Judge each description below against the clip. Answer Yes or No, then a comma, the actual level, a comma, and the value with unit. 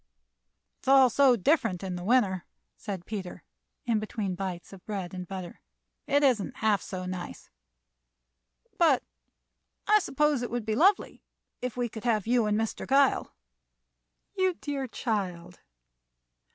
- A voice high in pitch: Yes, high, 220 Hz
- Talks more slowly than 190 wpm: Yes, average, 145 wpm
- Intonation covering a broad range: Yes, wide, 5.7 semitones